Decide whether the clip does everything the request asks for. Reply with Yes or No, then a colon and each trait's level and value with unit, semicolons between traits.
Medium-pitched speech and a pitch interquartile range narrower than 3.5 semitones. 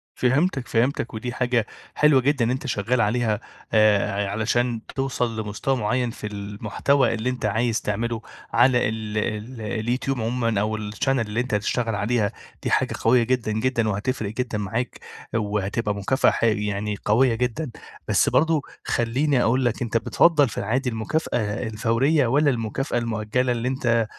No: low, 115 Hz; average, 3.0 semitones